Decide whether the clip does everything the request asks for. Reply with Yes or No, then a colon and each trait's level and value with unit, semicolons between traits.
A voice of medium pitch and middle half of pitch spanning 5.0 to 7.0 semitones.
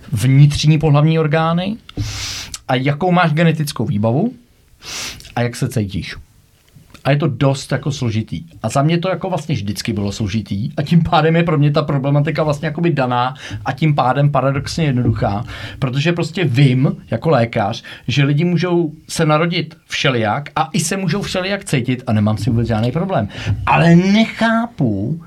Yes: medium, 145 Hz; wide, 5.6 semitones